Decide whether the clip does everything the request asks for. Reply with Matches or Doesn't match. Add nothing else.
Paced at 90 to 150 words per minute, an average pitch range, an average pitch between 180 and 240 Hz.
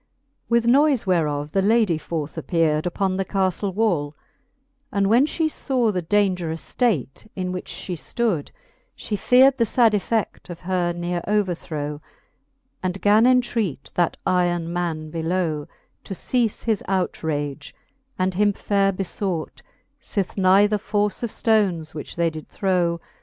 Matches